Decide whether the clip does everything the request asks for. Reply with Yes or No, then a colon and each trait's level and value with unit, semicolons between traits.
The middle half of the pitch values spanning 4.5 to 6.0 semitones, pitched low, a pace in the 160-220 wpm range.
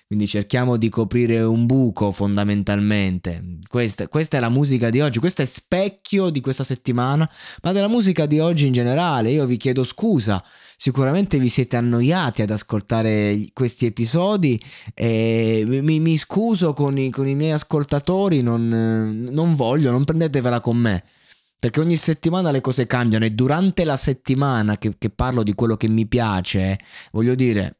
Yes: average, 5.1 semitones; low, 125 Hz; average, 165 wpm